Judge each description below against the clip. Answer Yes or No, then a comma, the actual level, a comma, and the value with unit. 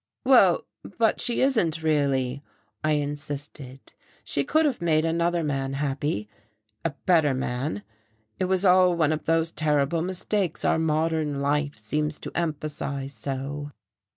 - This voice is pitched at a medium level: Yes, medium, 150 Hz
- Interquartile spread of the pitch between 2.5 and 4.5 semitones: Yes, average, 3.2 semitones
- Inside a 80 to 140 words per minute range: Yes, slow, 135 wpm